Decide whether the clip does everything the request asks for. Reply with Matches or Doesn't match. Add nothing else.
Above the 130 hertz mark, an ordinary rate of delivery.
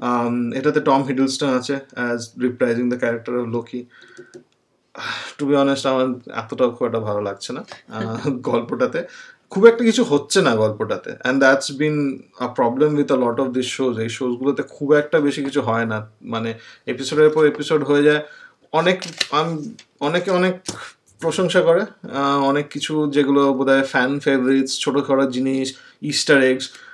Doesn't match